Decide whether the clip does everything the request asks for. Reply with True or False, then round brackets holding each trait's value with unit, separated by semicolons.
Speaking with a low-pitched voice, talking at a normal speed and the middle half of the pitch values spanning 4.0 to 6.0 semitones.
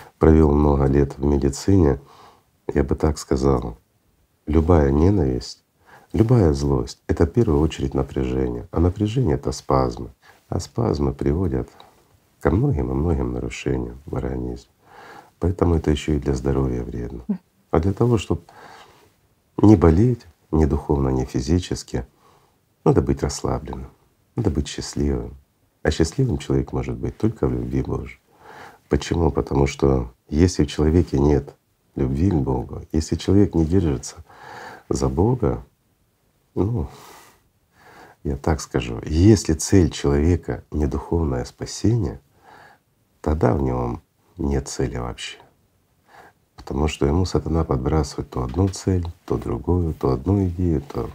True (75 Hz; 130 wpm; 4.5 semitones)